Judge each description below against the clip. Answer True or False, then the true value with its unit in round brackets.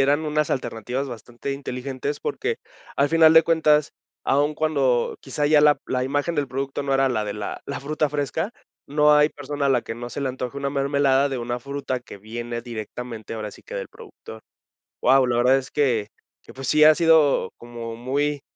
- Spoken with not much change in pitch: False (3.2 semitones)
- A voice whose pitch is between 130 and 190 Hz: True (135 Hz)